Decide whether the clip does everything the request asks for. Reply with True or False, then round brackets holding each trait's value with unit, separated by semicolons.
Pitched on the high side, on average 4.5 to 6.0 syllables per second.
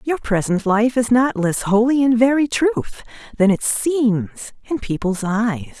False (230 Hz; 4.1 syllables/s)